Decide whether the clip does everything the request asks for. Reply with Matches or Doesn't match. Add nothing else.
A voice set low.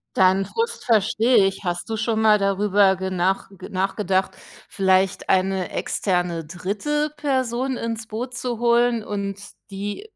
Doesn't match